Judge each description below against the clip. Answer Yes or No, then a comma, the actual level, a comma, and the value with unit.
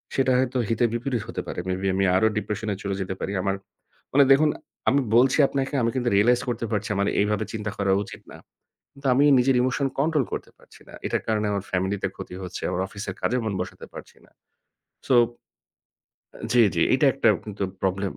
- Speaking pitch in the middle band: No, low, 110 Hz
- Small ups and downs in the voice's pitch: No, average, 4.5 semitones